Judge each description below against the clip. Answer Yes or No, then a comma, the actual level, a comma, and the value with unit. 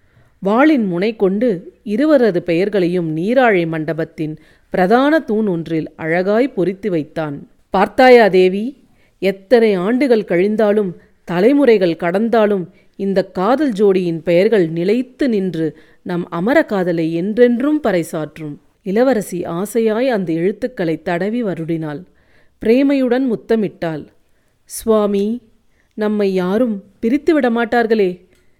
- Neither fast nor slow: Yes, average, 90 wpm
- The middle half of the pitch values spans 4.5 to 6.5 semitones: Yes, average, 5.2 semitones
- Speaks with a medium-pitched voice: No, high, 200 Hz